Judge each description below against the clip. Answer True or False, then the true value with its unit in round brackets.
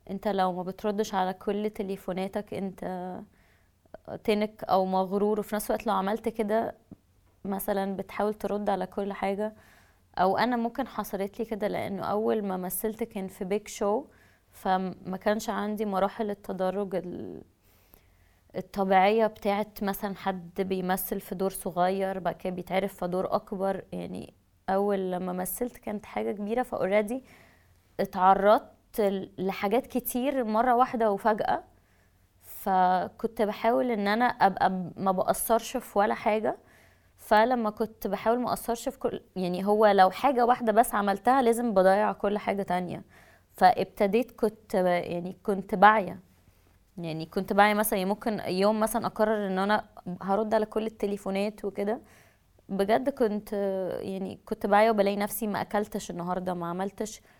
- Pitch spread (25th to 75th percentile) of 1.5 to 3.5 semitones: True (2.6 semitones)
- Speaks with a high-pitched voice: True (205 Hz)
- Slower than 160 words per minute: True (140 wpm)